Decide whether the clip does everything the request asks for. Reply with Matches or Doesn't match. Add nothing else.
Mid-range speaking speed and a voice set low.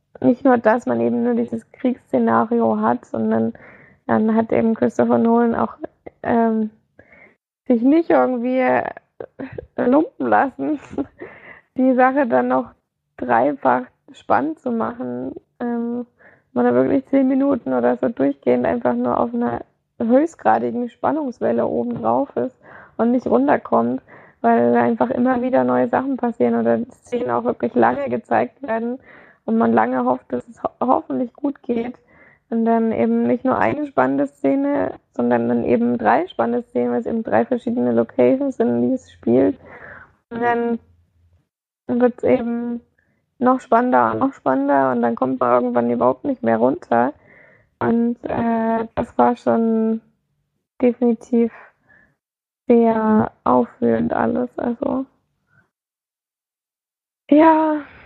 Doesn't match